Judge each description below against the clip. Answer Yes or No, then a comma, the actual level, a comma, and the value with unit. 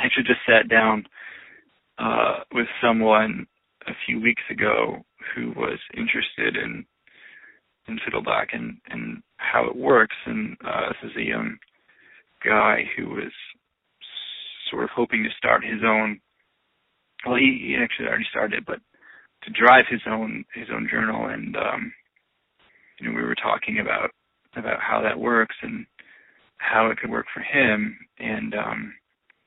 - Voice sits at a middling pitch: No, low, 115 Hz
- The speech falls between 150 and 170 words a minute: Yes, average, 155 wpm